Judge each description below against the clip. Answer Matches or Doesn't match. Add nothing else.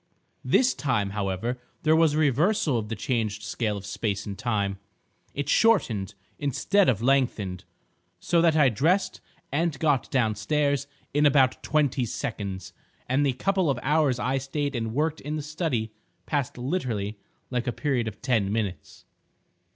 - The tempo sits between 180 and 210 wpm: Doesn't match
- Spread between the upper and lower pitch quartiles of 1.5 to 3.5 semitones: Doesn't match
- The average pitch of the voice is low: Matches